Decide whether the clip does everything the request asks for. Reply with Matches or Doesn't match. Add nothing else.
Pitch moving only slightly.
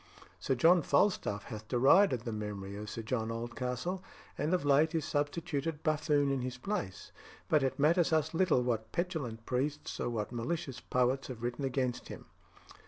Doesn't match